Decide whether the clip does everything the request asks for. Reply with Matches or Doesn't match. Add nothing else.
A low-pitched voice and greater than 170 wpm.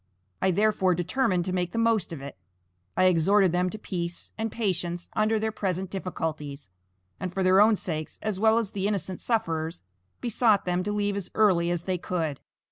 Doesn't match